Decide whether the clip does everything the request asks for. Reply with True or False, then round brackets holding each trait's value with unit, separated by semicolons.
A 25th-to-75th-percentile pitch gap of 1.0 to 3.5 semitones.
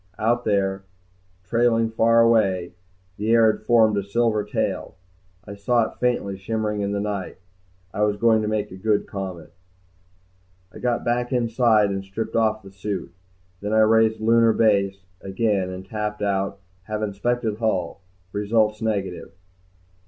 True (2.4 semitones)